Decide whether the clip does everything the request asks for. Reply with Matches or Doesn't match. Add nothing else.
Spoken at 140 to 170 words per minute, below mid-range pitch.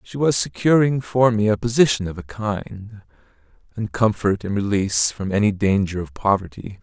Matches